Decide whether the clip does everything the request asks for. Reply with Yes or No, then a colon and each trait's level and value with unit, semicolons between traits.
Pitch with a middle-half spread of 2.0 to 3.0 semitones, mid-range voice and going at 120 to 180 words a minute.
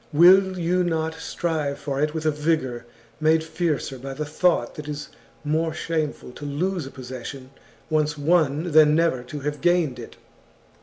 Yes: average, 2.7 semitones; medium, 155 Hz; average, 170 wpm